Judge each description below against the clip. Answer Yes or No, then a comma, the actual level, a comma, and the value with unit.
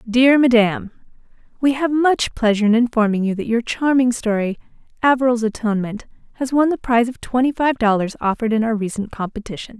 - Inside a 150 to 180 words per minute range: Yes, average, 170 wpm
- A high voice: Yes, high, 235 Hz